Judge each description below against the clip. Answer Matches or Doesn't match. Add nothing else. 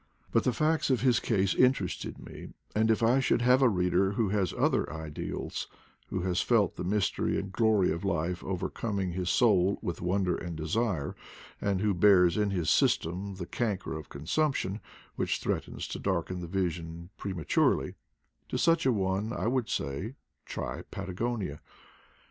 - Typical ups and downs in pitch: Matches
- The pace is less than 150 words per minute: Doesn't match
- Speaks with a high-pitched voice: Doesn't match